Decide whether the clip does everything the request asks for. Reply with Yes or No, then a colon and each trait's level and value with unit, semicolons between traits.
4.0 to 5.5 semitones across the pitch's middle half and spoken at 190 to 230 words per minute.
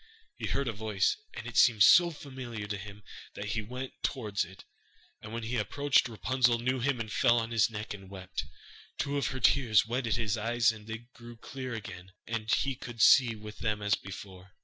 No: average, 2.9 semitones; fast, 205 wpm